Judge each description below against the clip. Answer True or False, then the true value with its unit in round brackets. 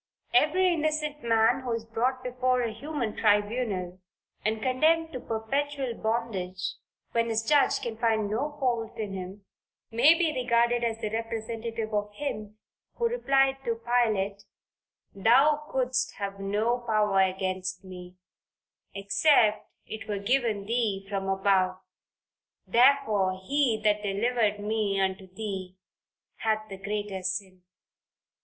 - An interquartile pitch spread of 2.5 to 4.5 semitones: True (4.0 semitones)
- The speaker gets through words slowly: True (130 wpm)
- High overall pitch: True (220 Hz)